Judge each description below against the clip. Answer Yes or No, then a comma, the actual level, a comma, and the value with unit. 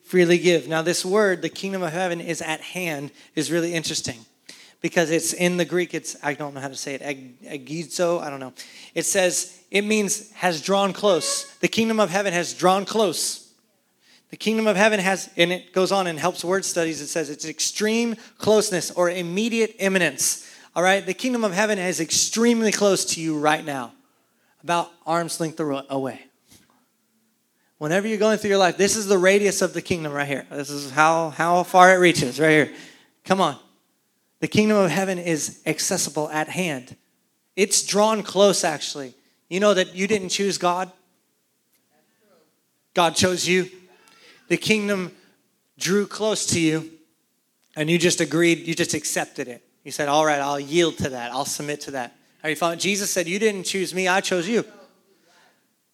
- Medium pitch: Yes, medium, 180 Hz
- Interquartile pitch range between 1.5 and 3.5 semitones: No, average, 3.9 semitones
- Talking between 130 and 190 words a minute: Yes, average, 180 wpm